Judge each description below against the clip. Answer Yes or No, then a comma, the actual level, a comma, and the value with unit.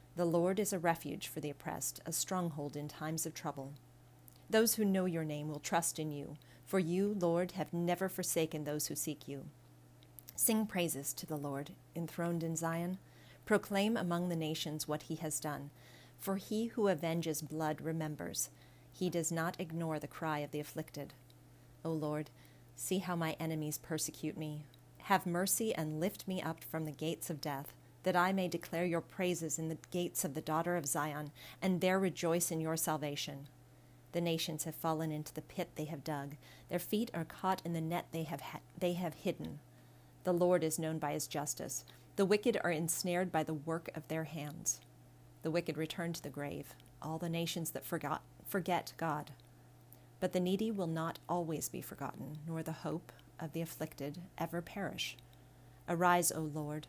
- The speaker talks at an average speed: Yes, average, 185 wpm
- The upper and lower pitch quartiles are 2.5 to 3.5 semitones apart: Yes, average, 2.9 semitones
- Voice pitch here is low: No, medium, 160 Hz